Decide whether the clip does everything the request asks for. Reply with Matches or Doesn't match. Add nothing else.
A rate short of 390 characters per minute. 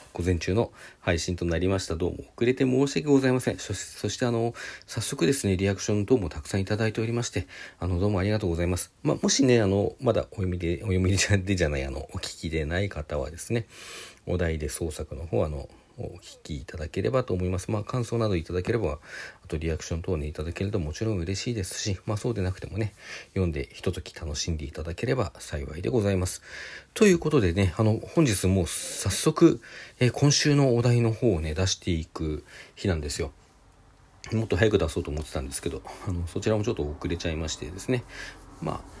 Doesn't match